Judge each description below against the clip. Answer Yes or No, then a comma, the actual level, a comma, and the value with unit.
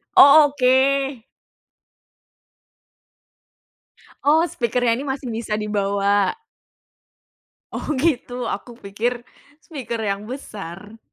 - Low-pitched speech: No, high, 240 Hz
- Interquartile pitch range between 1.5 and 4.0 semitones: No, average, 4.4 semitones